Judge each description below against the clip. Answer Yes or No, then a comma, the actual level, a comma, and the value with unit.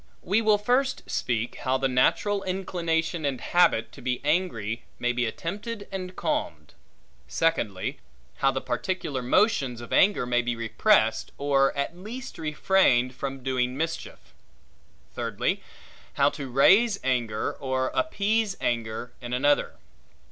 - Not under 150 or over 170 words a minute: No, slow, 135 wpm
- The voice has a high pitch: No, medium, 140 Hz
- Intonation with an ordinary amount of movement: No, wide, 7.6 semitones